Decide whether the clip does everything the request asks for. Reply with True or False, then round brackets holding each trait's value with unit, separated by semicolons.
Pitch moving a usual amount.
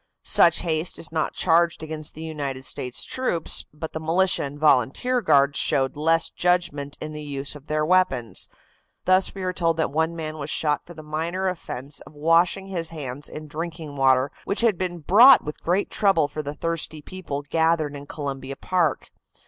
True (3.1 semitones)